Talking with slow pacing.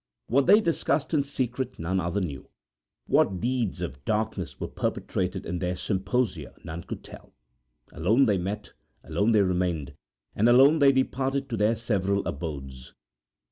No: average, 150 wpm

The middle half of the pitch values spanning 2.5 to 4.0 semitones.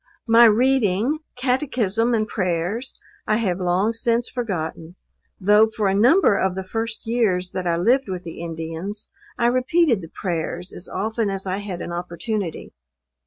No: average, 4.5 semitones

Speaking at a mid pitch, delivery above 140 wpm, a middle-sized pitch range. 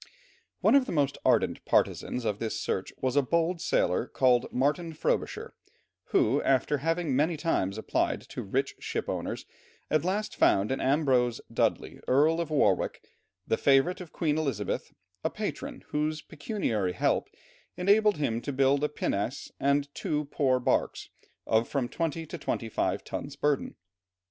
Yes: medium, 145 Hz; average, 155 wpm; average, 4.1 semitones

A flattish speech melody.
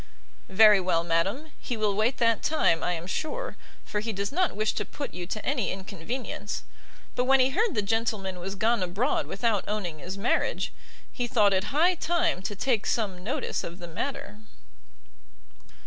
No: average, 5.1 semitones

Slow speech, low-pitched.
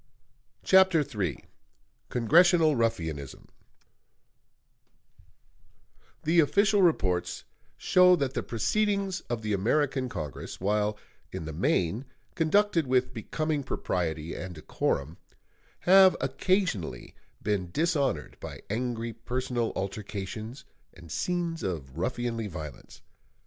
Yes: slow, 95 wpm; low, 120 Hz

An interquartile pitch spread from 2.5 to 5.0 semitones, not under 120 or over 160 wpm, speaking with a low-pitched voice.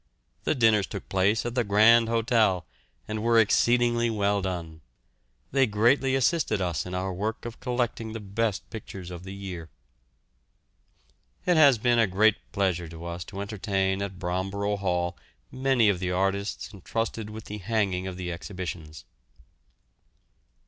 Yes: average, 3.7 semitones; average, 150 wpm; low, 100 Hz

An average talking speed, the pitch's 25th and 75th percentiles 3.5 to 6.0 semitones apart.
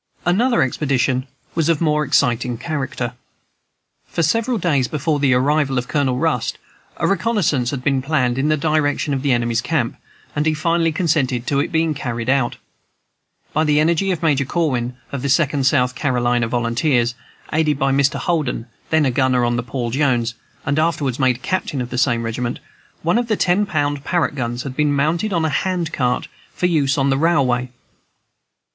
Yes: average, 180 wpm; average, 4.0 semitones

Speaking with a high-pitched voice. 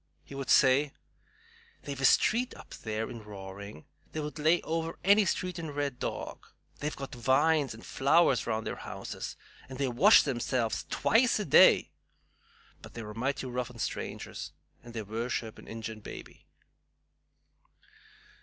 No: low, 135 Hz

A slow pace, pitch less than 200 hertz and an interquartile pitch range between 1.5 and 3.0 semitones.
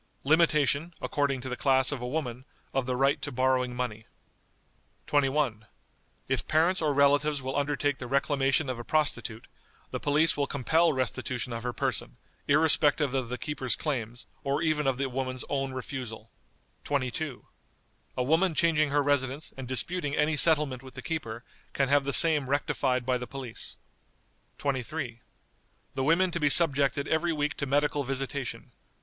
No: average, 160 wpm; medium, 140 Hz; narrow, 2.6 semitones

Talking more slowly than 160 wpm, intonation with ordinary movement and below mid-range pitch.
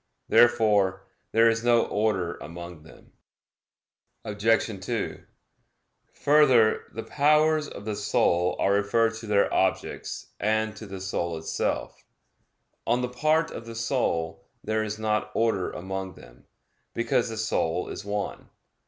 Yes: slow, 135 wpm; average, 3.4 semitones; low, 110 Hz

